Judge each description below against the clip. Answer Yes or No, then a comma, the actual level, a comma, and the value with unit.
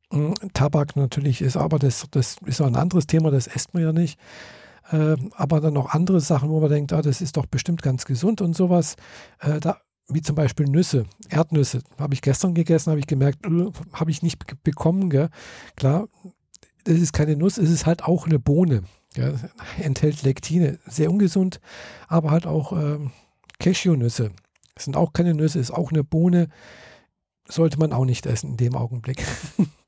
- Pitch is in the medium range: Yes, medium, 155 Hz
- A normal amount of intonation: Yes, average, 3.4 semitones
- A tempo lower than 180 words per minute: Yes, average, 170 wpm